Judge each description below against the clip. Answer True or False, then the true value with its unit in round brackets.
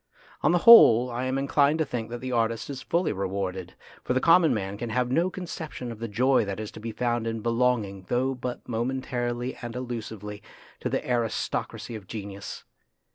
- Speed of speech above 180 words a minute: True (195 wpm)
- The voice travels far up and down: False (3.0 semitones)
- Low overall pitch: True (120 Hz)